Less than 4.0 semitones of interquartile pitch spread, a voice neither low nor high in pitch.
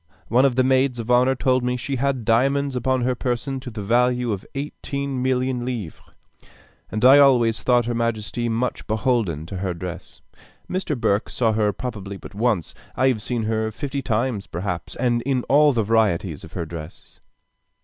No: average, 3.2 semitones; low, 120 Hz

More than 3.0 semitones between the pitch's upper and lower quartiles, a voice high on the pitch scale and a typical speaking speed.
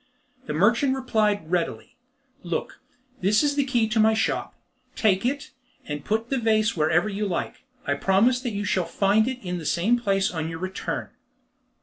Yes: average, 4.8 semitones; high, 210 Hz; average, 180 wpm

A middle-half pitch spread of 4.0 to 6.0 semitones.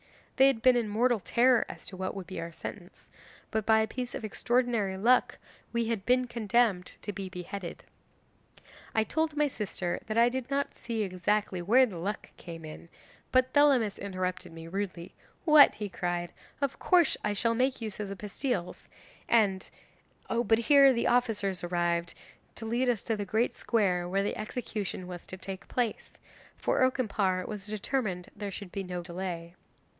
Yes: average, 4.6 semitones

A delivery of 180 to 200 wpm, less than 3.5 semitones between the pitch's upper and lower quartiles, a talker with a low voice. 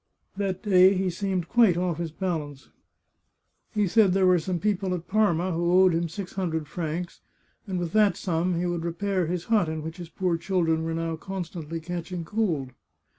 No: average, 185 wpm; narrow, 2.4 semitones; medium, 175 Hz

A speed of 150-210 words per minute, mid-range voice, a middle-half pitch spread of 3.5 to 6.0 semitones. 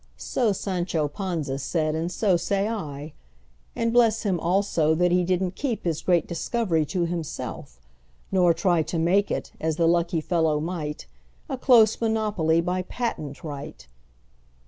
No: slow, 135 wpm; medium, 170 Hz; average, 4.0 semitones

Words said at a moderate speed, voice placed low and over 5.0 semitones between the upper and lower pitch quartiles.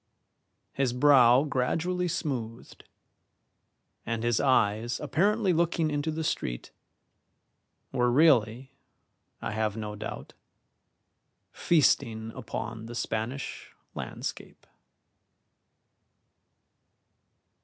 No: slow, 80 wpm; low, 125 Hz; wide, 5.4 semitones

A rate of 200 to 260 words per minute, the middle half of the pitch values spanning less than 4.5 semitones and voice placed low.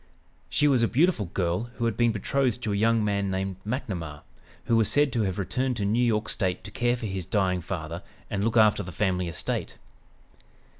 Yes: fast, 205 wpm; average, 4.0 semitones; low, 105 Hz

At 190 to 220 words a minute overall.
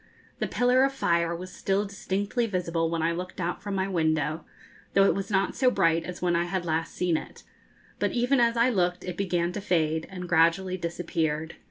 Yes: fast, 205 wpm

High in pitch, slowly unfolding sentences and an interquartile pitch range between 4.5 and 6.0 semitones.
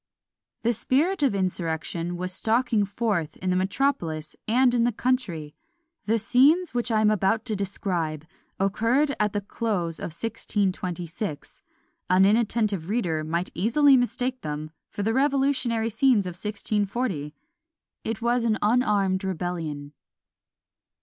Yes: high, 210 Hz; slow, 130 wpm; average, 5.2 semitones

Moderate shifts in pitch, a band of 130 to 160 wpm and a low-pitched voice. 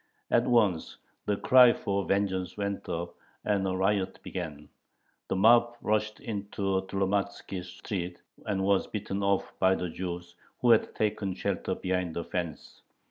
No: narrow, 2.2 semitones; average, 145 wpm; very low, 95 Hz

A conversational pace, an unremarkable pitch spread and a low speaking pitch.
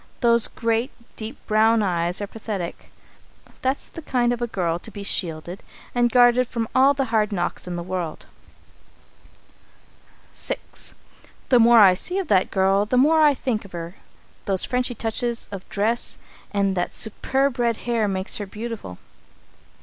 No: average, 160 wpm; average, 4.2 semitones; high, 220 Hz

